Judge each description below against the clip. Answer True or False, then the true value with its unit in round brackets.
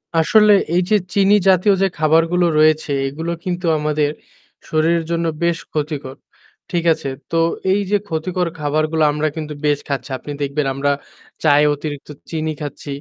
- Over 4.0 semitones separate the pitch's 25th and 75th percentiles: False (2.5 semitones)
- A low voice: False (155 Hz)